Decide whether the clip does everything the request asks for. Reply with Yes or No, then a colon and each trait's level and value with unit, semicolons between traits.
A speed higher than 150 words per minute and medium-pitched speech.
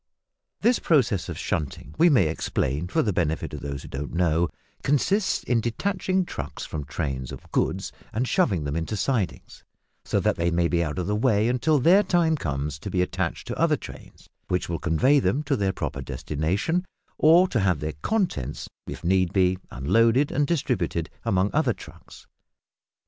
No: average, 180 wpm; very low, 95 Hz